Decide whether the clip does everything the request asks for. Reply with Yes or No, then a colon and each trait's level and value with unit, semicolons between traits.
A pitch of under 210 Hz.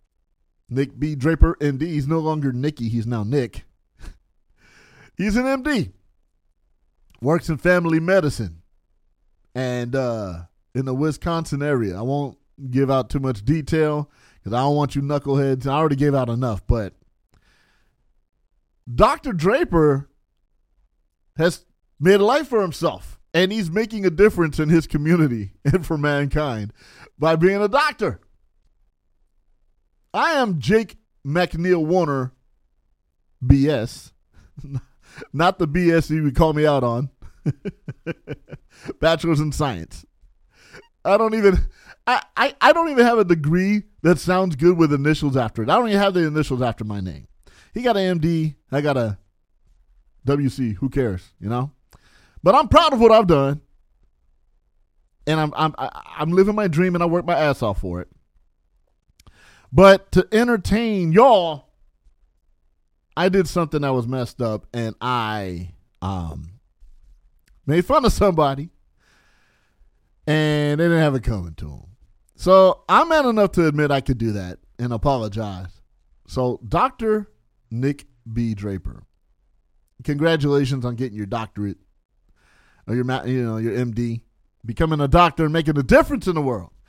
Yes: medium, 140 Hz